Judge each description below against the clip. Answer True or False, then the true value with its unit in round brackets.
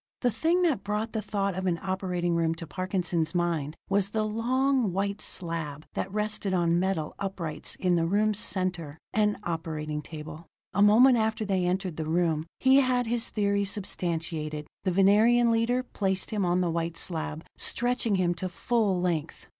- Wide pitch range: False (4.2 semitones)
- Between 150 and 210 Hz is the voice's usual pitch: True (190 Hz)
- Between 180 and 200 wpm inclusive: False (170 wpm)